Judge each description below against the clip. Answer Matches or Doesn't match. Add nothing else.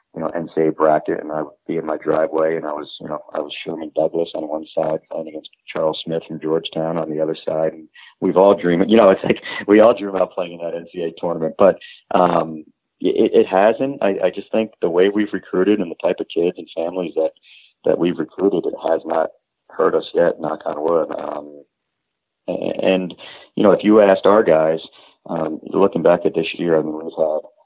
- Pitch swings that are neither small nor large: Doesn't match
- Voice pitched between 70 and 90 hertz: Matches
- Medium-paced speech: Doesn't match